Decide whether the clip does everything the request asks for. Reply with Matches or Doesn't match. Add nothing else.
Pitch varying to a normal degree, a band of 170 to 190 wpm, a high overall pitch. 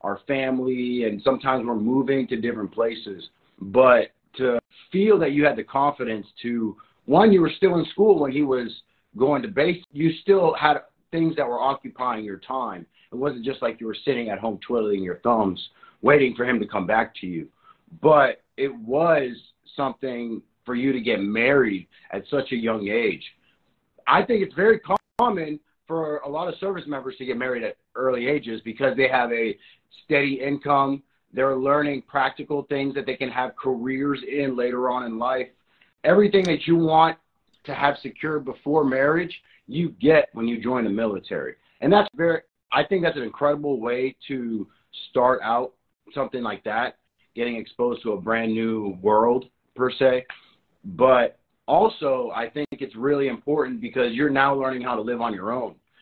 Doesn't match